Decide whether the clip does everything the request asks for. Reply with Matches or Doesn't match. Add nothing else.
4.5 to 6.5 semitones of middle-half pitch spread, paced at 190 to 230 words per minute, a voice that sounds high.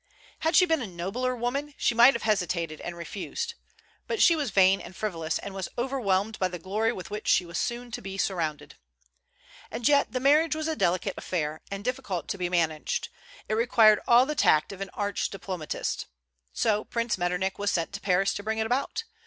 Matches